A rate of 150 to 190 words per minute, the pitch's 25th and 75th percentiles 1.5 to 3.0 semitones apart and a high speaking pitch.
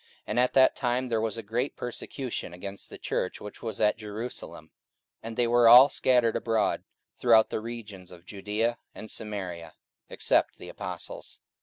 No: average, 165 wpm; narrow, 2.6 semitones; low, 115 Hz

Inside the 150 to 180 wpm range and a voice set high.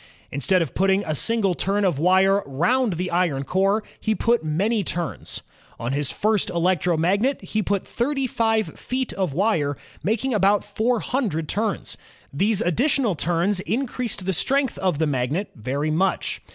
Yes: average, 160 wpm; high, 195 Hz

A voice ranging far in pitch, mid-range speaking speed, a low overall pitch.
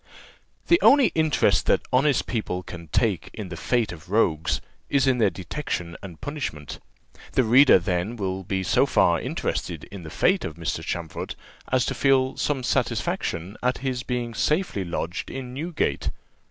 Yes: wide, 7.1 semitones; average, 165 wpm; low, 115 Hz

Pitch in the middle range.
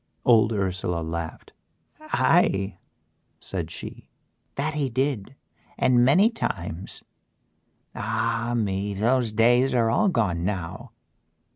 No: low, 115 Hz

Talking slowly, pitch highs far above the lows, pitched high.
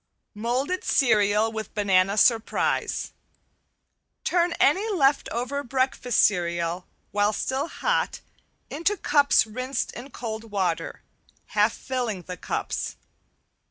No: slow, 105 wpm; average, 5.0 semitones; high, 235 Hz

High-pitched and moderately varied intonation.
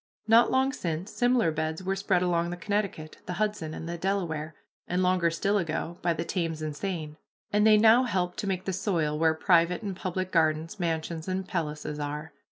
No: medium, 175 Hz; average, 3.5 semitones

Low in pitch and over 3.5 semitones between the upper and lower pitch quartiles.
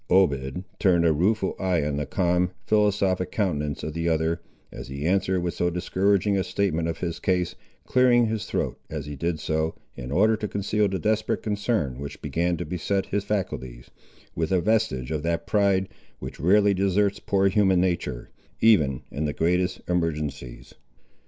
Yes: very low, 90 Hz; average, 4.1 semitones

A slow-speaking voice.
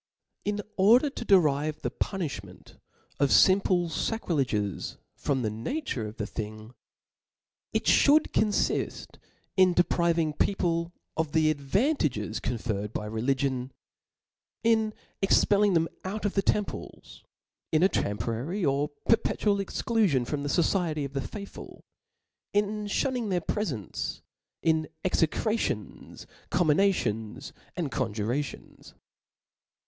Yes: slow, 120 wpm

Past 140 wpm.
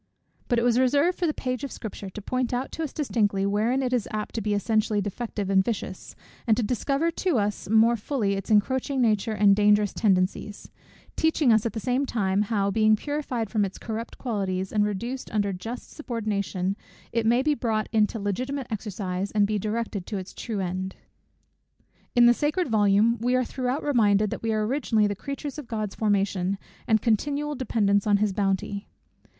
Yes: average, 190 wpm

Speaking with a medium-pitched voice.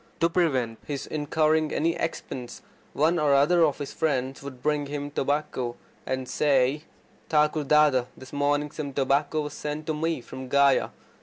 Yes: medium, 145 Hz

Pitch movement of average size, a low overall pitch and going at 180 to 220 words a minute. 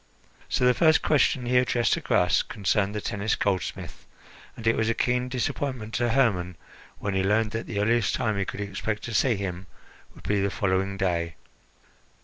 Yes: average, 3.6 semitones; low, 105 Hz; average, 185 wpm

